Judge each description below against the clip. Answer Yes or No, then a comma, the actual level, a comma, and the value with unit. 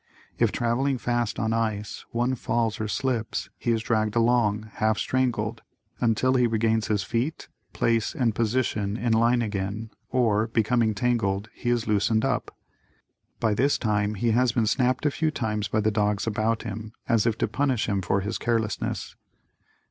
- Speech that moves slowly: No, average, 170 wpm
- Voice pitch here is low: Yes, low, 115 Hz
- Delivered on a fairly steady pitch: Yes, narrow, 2.0 semitones